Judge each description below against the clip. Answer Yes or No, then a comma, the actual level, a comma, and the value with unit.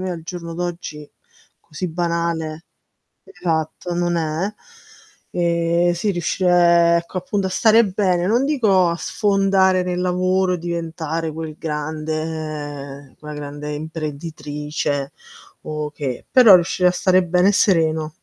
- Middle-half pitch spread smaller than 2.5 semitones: No, average, 2.8 semitones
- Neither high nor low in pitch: Yes, medium, 170 Hz